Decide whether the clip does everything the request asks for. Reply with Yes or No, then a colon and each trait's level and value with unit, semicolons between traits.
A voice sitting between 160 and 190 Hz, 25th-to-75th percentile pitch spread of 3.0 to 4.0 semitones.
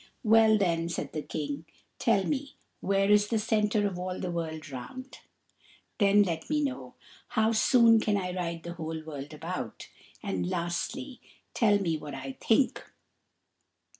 No: medium, 185 Hz; average, 5.2 semitones